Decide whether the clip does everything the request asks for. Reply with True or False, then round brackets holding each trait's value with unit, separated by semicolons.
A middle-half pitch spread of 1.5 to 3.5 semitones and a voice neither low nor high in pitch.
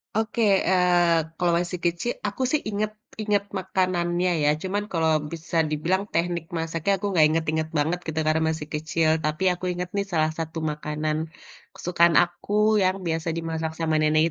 True (2.4 semitones; 170 Hz)